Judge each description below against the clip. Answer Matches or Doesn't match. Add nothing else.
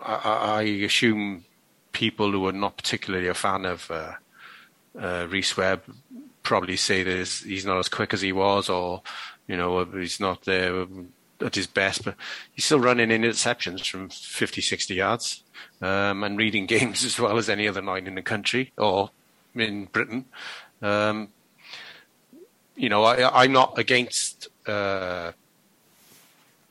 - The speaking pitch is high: Doesn't match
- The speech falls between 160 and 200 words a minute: Doesn't match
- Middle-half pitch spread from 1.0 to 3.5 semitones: Matches